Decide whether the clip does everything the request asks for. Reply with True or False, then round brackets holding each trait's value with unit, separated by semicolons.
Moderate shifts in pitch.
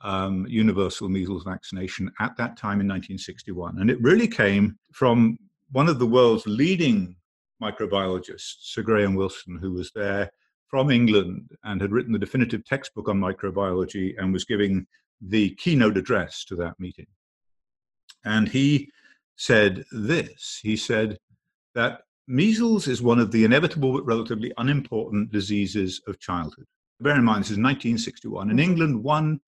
True (4.0 semitones)